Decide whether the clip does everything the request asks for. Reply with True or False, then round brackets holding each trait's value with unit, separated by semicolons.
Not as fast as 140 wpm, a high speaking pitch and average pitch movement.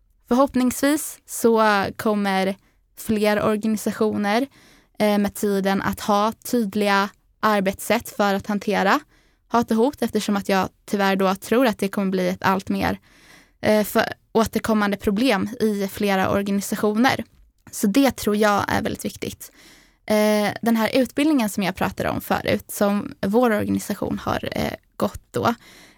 False (130 wpm; 210 Hz; 2.1 semitones)